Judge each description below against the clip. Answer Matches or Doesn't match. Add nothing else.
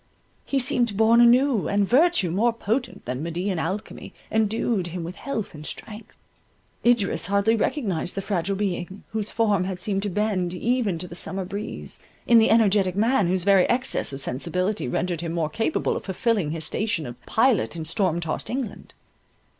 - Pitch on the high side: Matches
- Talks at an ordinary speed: Matches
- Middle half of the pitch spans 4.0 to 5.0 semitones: Matches